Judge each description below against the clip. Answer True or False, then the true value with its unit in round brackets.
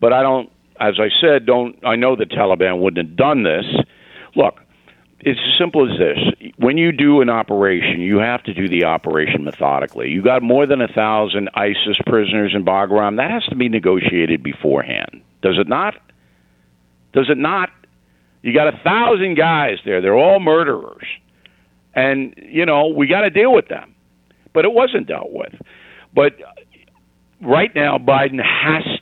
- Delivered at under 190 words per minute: True (170 wpm)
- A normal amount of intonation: False (7.9 semitones)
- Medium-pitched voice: False (110 Hz)